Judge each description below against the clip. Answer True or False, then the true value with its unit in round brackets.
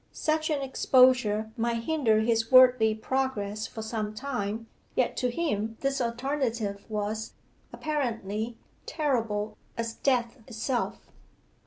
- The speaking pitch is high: True (230 Hz)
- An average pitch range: True (3.3 semitones)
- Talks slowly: True (115 wpm)